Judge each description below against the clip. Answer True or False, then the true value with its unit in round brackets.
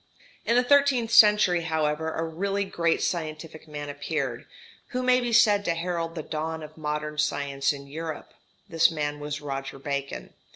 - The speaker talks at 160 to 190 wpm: True (165 wpm)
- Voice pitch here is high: False (160 Hz)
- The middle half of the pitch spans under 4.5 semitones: True (3.8 semitones)